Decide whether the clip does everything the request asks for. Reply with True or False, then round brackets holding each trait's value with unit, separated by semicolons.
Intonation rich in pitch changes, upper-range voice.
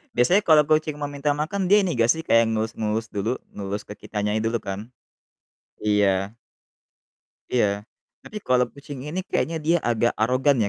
False (6.0 semitones; 120 Hz)